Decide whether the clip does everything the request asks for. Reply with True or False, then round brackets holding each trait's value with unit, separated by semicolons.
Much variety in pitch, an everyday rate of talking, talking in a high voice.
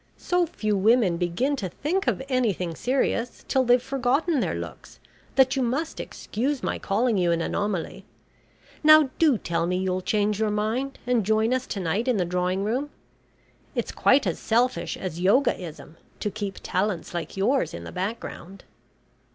True (5.8 semitones; 170 wpm; 215 Hz)